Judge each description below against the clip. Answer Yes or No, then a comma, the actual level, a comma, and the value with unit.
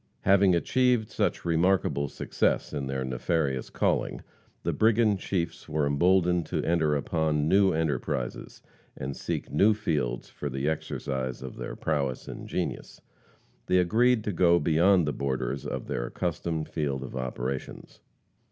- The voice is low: Yes, very low, 80 Hz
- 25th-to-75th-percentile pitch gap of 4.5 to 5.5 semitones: Yes, average, 5.2 semitones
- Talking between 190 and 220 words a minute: No, average, 145 wpm